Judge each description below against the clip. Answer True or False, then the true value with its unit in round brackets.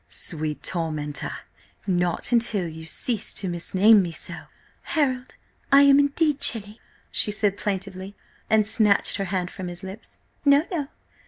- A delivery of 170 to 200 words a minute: False (145 wpm)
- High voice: True (200 Hz)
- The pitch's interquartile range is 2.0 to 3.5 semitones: False (5.3 semitones)